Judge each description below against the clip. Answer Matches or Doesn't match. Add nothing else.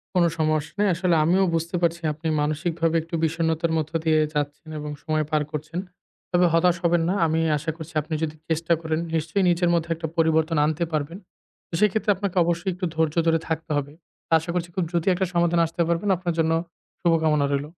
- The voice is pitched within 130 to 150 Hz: Doesn't match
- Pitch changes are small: Matches